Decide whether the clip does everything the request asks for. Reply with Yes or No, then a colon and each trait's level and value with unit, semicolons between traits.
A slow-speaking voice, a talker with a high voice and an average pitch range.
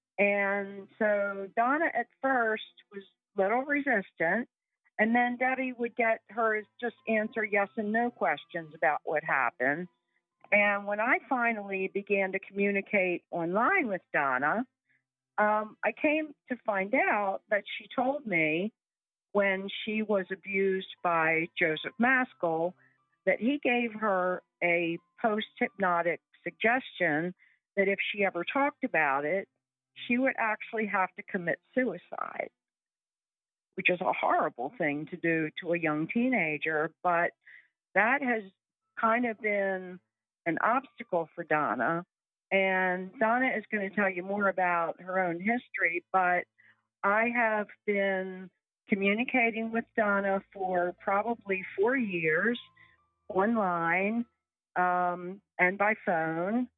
Yes: slow, 130 wpm; high, 200 Hz; average, 4.3 semitones